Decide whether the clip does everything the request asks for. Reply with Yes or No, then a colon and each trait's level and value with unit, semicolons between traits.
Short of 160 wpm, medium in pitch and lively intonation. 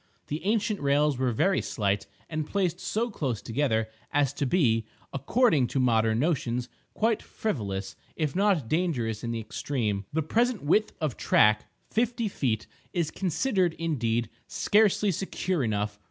Yes: average, 140 wpm; medium, 145 Hz; wide, 8.6 semitones